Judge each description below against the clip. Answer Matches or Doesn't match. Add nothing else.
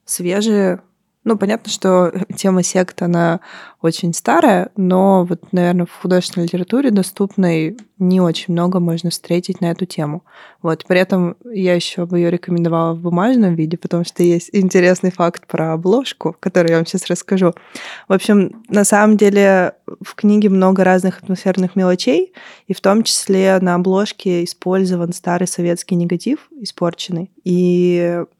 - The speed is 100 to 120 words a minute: Doesn't match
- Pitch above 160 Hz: Matches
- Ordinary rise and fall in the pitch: Doesn't match